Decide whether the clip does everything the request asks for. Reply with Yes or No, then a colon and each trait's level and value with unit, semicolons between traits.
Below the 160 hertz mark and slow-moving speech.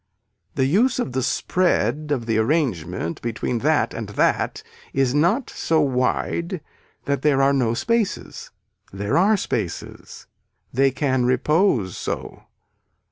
Yes: low, 135 Hz; slow, 130 wpm